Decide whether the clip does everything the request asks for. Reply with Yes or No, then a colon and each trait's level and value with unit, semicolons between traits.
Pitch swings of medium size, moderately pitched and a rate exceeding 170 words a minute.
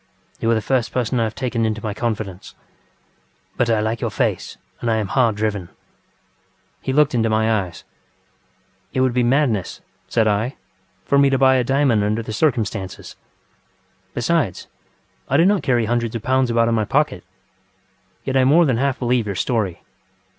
No: average, 3.2 semitones; low, 115 Hz; average, 180 wpm